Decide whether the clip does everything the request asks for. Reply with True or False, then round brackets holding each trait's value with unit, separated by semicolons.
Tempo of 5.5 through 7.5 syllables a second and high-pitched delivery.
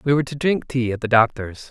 False (6.2 syllables/s; 125 Hz)